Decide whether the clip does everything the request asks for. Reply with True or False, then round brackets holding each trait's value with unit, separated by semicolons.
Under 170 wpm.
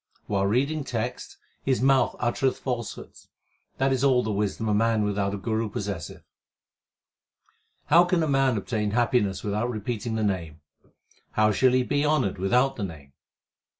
True (150 wpm)